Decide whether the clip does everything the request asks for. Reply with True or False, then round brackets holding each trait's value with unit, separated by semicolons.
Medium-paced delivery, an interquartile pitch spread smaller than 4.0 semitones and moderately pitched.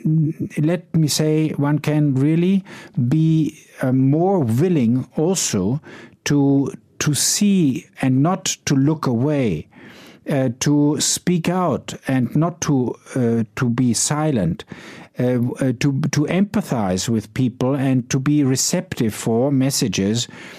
False (120 wpm; 3.4 semitones; 145 Hz)